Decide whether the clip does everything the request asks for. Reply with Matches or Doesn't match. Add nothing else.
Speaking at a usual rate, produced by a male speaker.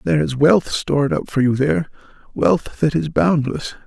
Matches